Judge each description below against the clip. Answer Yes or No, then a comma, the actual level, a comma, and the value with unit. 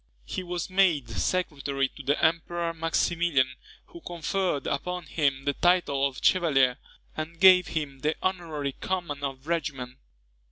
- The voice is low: No, medium, 160 Hz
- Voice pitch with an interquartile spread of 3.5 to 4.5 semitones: Yes, average, 4.1 semitones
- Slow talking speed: No, average, 145 wpm